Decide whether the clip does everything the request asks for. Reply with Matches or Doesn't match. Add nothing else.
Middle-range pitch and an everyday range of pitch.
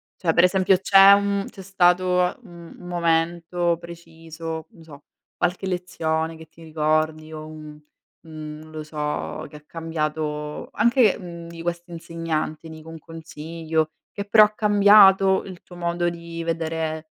Doesn't match